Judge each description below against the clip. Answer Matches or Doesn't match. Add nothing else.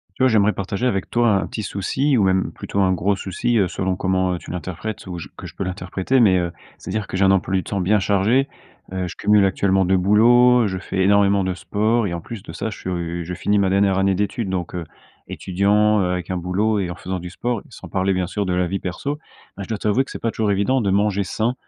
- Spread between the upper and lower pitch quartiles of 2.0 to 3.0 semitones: Matches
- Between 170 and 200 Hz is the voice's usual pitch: Doesn't match